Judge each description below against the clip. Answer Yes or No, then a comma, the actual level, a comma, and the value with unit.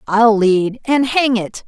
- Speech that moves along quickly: No, average, 180 wpm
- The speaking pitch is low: No, high, 230 Hz